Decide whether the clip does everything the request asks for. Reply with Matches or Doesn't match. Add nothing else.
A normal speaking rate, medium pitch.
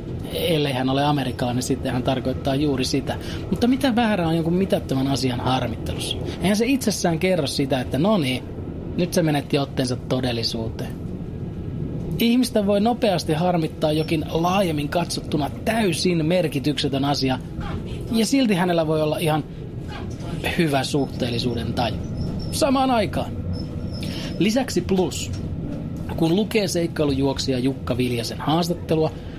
Matches